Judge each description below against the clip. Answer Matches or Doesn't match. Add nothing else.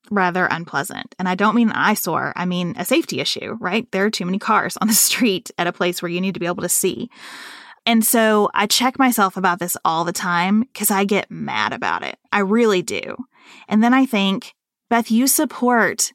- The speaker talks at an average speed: Doesn't match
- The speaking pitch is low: Doesn't match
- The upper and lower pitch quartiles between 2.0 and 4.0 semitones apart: Doesn't match